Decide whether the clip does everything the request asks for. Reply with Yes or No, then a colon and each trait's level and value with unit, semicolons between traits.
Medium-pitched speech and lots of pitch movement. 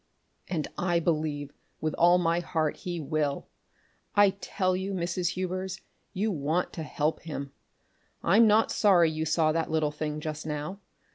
No: medium, 165 Hz; average, 3.2 semitones